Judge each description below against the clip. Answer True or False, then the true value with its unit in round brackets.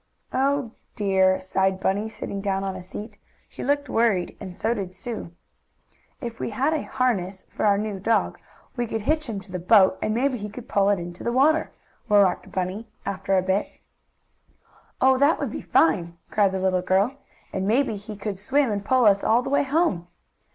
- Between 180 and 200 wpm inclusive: True (195 wpm)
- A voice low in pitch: False (205 Hz)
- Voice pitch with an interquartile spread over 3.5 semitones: True (4.3 semitones)